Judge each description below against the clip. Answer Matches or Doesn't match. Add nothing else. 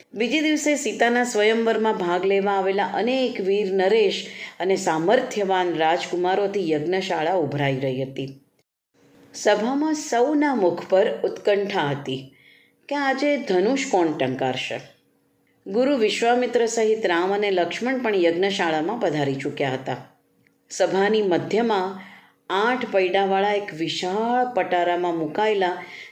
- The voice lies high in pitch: Matches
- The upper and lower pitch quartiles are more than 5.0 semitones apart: Matches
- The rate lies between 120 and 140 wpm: Doesn't match